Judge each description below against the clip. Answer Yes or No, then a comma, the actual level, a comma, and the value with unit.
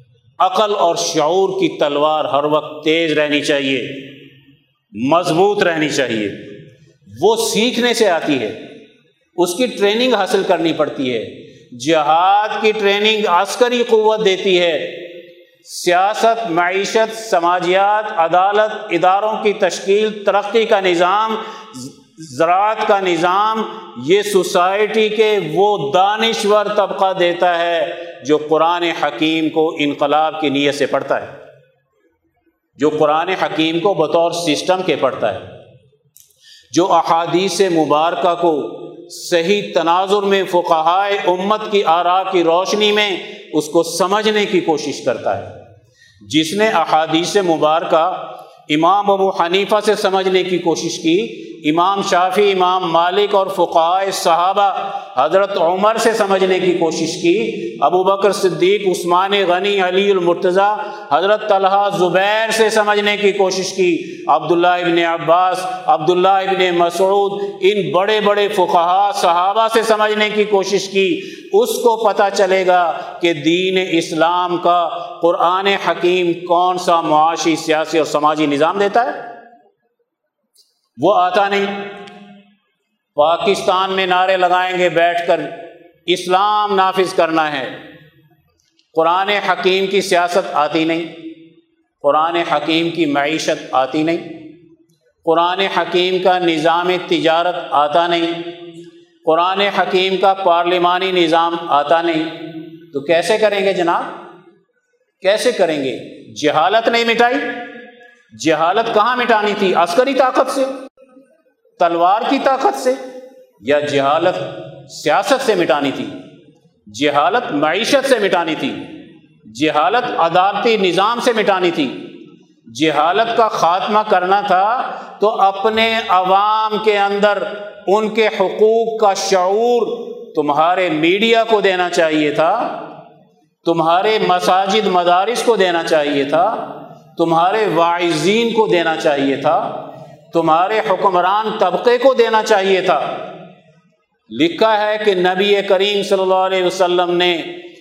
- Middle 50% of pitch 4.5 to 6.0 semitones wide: No, average, 4.1 semitones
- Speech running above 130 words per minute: No, average, 120 wpm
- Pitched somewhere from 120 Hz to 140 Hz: No, medium, 185 Hz